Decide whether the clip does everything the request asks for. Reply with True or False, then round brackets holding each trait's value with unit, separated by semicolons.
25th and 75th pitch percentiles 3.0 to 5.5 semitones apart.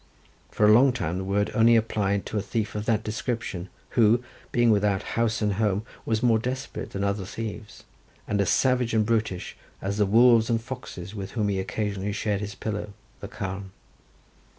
False (2.4 semitones)